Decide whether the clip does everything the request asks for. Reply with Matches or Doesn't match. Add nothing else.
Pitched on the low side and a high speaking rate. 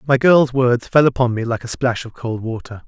Matches